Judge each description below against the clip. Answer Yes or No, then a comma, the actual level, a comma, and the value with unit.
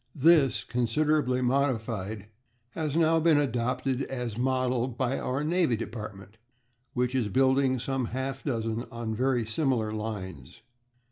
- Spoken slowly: Yes, slow, 125 wpm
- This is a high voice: No, low, 125 Hz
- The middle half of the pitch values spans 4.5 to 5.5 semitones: No, average, 3.1 semitones